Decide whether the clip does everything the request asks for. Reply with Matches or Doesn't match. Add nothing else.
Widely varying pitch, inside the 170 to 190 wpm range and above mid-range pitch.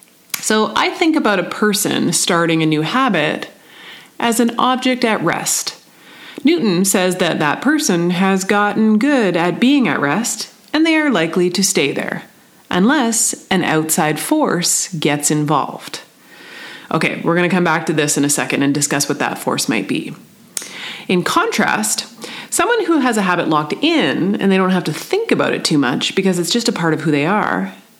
Matches